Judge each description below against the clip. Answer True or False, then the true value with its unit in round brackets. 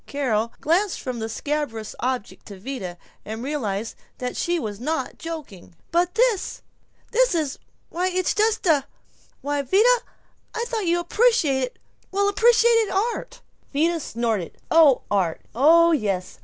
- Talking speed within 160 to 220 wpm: False (140 wpm)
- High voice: True (300 Hz)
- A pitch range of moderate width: False (8.1 semitones)